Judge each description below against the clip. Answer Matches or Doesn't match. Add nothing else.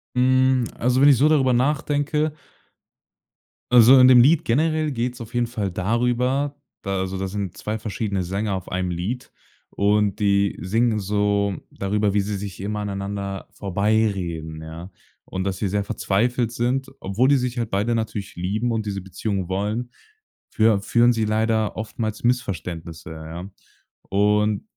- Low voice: Matches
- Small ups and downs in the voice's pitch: Doesn't match